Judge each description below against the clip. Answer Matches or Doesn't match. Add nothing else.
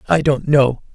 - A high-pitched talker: Doesn't match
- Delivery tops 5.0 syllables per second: Doesn't match